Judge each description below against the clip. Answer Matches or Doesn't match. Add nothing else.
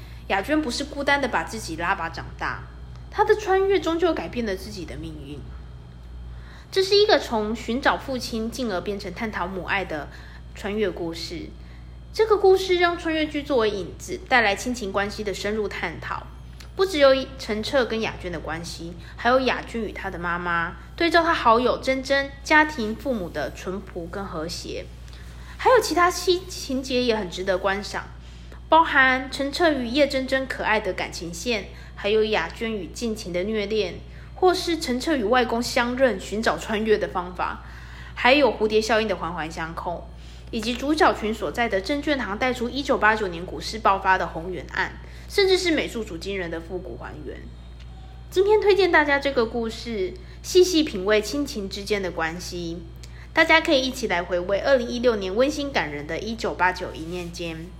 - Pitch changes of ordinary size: Doesn't match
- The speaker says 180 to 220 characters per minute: Doesn't match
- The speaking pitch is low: Doesn't match